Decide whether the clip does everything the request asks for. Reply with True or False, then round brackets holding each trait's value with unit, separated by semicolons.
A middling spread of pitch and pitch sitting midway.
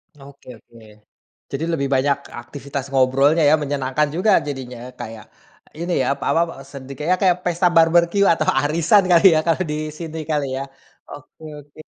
True (3.4 semitones; 145 Hz)